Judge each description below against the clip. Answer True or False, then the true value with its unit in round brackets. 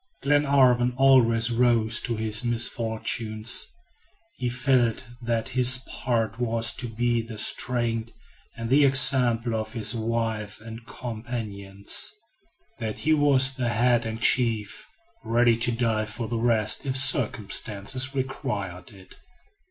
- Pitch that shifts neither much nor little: False (2.0 semitones)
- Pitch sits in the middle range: False (115 Hz)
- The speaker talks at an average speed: False (125 wpm)